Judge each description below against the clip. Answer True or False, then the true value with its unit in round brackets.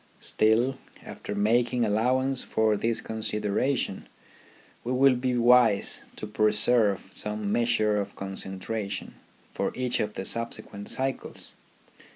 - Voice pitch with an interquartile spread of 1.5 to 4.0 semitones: True (2.9 semitones)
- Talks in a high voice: False (110 Hz)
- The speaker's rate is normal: False (115 wpm)